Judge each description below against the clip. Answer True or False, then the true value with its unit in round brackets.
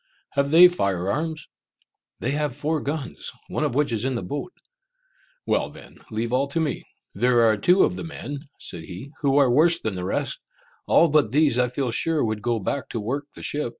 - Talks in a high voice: False (140 Hz)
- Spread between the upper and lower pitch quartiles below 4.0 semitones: False (4.7 semitones)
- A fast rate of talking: True (210 wpm)